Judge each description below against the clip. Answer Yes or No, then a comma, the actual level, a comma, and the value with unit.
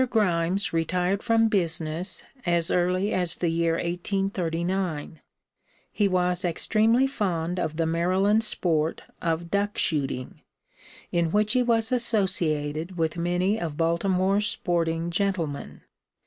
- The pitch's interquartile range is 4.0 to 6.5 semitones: No, average, 3.2 semitones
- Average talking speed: No, slow, 120 wpm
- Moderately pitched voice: Yes, medium, 180 Hz